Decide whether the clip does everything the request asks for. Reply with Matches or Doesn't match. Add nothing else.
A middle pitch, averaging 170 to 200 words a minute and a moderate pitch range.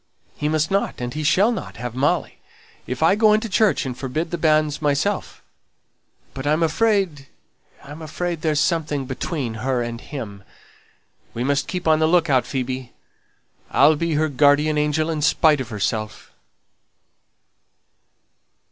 Doesn't match